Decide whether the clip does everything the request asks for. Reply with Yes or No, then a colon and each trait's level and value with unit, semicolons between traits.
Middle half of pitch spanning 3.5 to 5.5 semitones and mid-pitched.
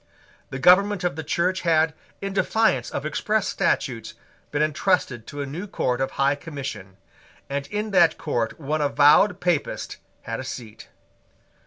Yes: average, 5.1 semitones; medium, 155 Hz